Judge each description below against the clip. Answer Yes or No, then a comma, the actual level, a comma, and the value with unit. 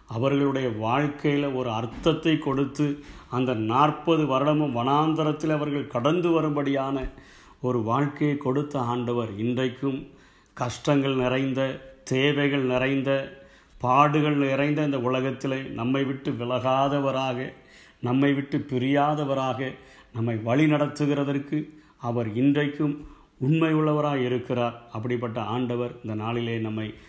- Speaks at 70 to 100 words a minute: Yes, average, 95 wpm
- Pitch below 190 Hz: Yes, low, 135 Hz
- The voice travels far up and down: No, average, 2.7 semitones